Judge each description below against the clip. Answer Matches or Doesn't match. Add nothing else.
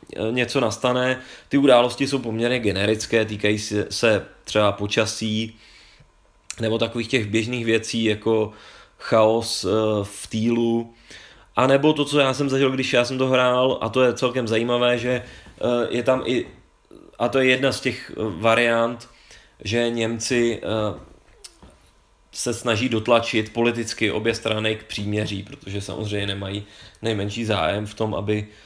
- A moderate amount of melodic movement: Doesn't match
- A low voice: Matches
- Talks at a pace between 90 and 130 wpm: Doesn't match